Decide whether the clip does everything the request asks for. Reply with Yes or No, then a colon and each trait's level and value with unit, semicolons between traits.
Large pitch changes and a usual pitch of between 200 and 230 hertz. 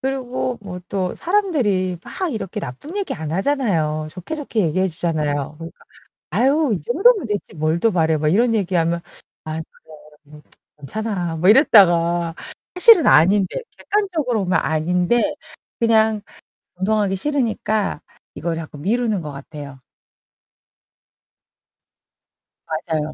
No: wide, 6.9 semitones; high, 190 Hz